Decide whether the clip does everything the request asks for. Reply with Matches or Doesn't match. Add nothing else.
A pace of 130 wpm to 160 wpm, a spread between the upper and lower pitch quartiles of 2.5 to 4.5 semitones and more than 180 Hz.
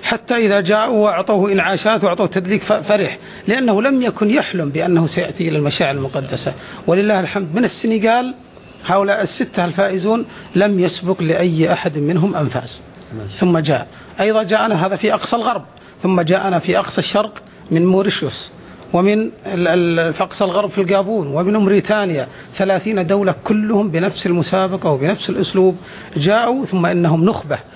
Matches